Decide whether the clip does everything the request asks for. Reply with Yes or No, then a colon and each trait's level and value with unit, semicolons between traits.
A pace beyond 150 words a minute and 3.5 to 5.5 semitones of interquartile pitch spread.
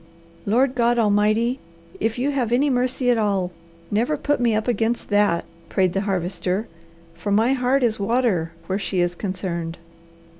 Yes: average, 160 wpm; average, 4.3 semitones